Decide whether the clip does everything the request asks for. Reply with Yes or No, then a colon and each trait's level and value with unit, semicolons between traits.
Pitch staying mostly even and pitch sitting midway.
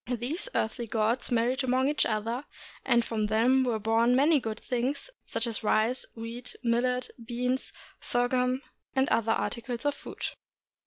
No: narrow, 2.1 semitones; high, 245 Hz